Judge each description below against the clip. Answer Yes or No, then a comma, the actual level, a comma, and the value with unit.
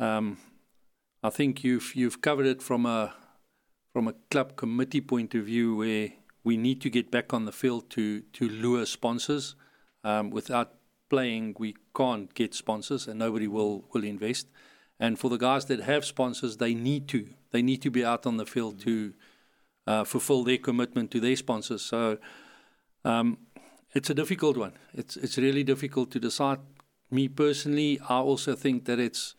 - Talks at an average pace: Yes, average, 175 wpm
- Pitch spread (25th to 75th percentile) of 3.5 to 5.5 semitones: No, average, 3.1 semitones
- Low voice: Yes, low, 125 Hz